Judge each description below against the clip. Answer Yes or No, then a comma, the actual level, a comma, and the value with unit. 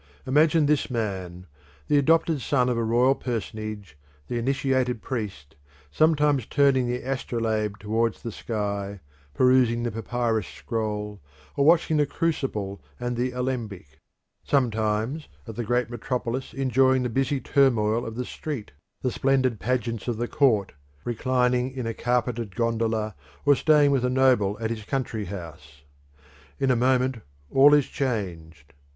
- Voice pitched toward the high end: No, low, 120 Hz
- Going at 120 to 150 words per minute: Yes, average, 145 wpm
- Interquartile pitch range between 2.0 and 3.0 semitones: No, average, 3.6 semitones